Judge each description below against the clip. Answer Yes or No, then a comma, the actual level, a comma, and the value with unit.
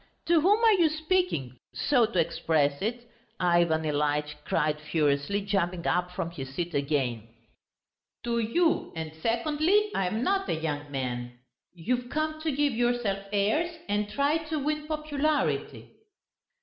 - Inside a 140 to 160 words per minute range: Yes, average, 145 wpm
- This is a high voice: Yes, high, 205 Hz